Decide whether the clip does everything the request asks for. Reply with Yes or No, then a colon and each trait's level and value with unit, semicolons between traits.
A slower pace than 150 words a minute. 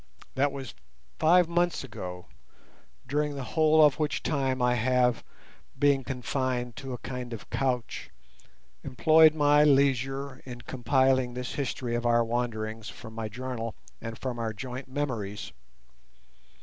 Yes: slow, 135 wpm